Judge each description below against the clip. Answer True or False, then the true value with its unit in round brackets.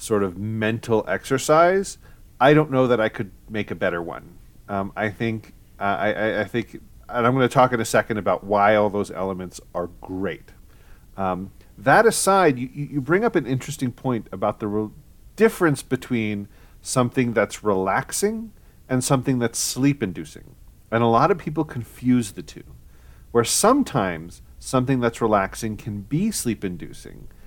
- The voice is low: True (115 Hz)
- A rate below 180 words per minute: True (160 wpm)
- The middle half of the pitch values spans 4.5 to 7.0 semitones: True (5.0 semitones)